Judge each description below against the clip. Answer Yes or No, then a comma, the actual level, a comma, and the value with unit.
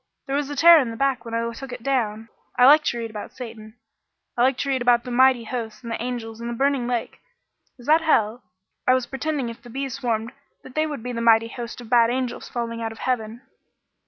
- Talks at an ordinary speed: No, fast, 245 wpm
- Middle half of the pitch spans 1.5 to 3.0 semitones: Yes, narrow, 2.6 semitones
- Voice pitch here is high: Yes, high, 240 Hz